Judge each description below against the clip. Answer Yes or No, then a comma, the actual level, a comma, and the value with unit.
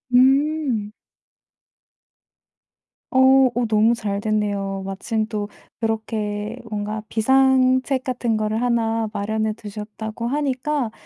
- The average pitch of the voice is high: Yes, high, 225 Hz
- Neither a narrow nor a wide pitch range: Yes, average, 3.4 semitones